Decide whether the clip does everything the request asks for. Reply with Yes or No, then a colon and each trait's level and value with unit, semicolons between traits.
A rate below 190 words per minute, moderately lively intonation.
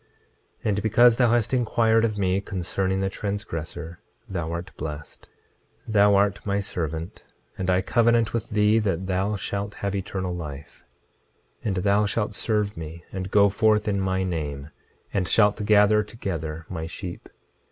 Yes: average, 160 wpm; average, 3.1 semitones